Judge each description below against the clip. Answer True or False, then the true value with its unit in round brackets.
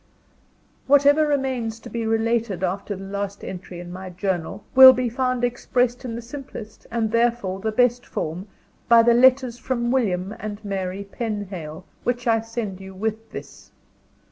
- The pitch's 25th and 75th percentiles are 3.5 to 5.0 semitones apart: True (4.0 semitones)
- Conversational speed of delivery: True (160 wpm)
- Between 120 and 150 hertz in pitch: False (225 Hz)